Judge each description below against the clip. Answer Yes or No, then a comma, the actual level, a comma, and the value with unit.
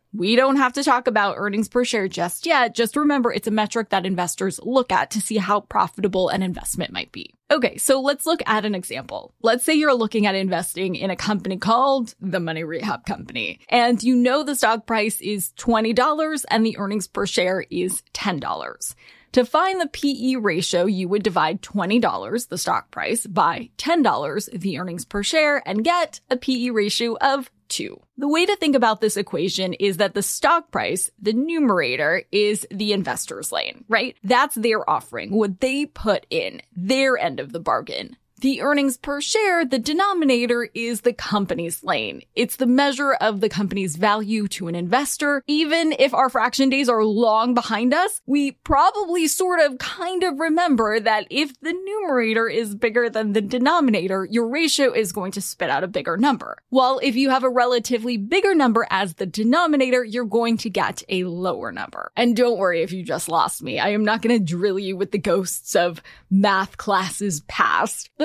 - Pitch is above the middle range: Yes, high, 230 Hz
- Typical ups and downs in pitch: Yes, average, 5.0 semitones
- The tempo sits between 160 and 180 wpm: No, average, 190 wpm